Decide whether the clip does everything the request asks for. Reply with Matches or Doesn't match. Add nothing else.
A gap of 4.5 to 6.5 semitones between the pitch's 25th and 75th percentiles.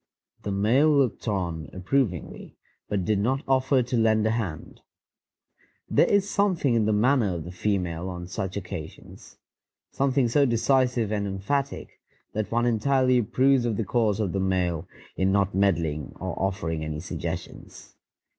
Matches